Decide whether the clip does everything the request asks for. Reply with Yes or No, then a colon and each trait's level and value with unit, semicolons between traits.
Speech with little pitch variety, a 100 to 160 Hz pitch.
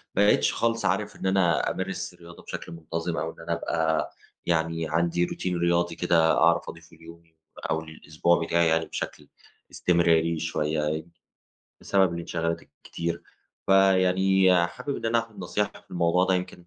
No: narrow, 1.9 semitones; very low, 85 Hz